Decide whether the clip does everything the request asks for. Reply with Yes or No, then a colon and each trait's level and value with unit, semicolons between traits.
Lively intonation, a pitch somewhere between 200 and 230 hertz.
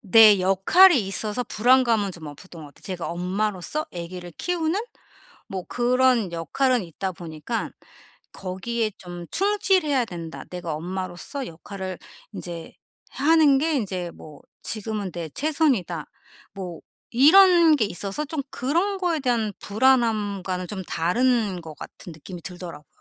Yes: wide, 6.7 semitones; high, 205 Hz